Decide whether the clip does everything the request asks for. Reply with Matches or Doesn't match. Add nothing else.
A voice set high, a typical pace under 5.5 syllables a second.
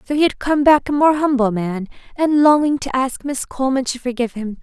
Doesn't match